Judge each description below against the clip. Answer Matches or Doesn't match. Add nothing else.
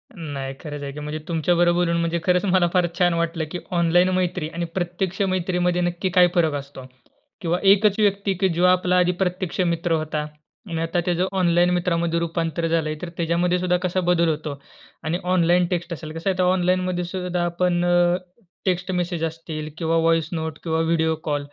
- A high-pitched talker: Doesn't match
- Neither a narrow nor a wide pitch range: Doesn't match